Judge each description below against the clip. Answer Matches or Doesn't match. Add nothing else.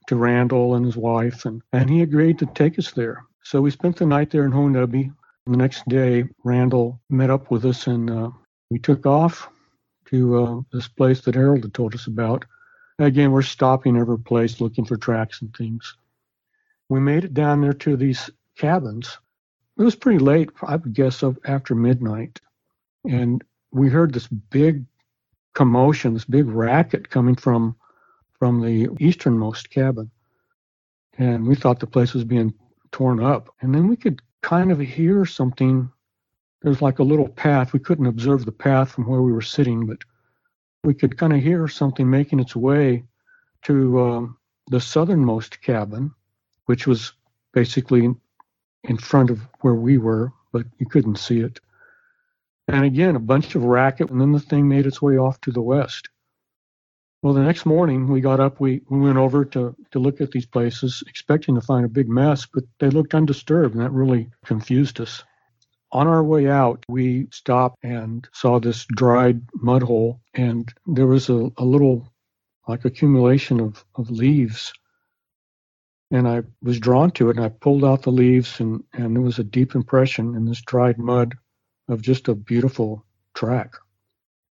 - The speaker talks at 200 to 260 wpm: Doesn't match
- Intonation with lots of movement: Doesn't match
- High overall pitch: Doesn't match